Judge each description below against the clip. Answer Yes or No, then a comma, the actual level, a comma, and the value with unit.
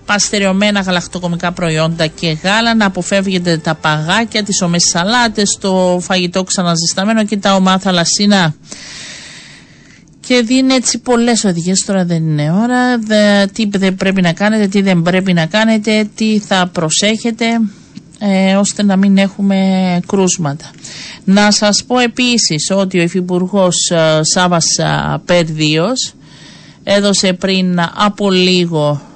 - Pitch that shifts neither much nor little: Yes, average, 3.1 semitones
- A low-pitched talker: No, high, 190 Hz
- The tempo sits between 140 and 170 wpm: No, average, 125 wpm